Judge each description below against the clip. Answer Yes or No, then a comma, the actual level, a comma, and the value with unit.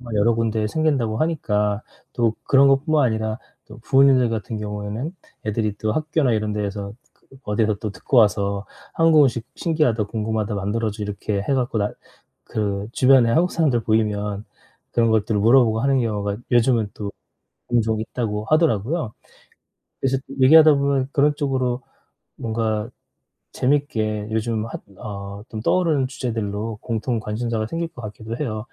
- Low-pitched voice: Yes, low, 115 Hz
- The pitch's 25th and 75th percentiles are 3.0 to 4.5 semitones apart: Yes, average, 4.0 semitones